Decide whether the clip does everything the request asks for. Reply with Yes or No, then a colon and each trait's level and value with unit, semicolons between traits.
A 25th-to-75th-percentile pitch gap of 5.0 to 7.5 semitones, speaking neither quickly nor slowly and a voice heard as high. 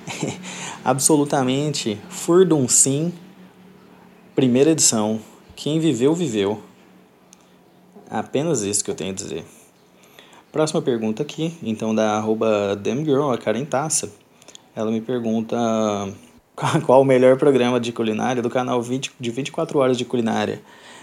No: wide, 5.5 semitones; average, 130 wpm; low, 130 Hz